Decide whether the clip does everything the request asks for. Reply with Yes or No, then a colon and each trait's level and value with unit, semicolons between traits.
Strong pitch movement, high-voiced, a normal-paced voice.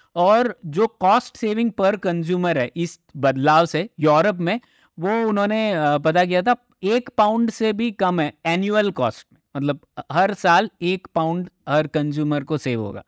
No: wide, 5.8 semitones; medium, 175 Hz; average, 165 wpm